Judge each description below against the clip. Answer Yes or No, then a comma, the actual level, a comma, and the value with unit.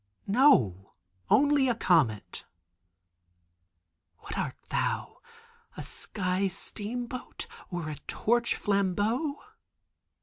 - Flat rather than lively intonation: No, wide, 5.6 semitones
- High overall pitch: Yes, high, 205 Hz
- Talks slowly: Yes, slow, 75 wpm